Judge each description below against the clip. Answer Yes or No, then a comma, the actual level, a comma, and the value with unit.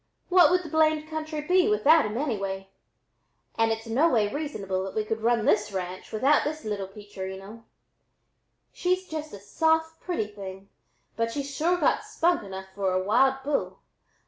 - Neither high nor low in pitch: No, high, 230 Hz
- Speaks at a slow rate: No, average, 170 wpm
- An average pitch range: No, wide, 7.6 semitones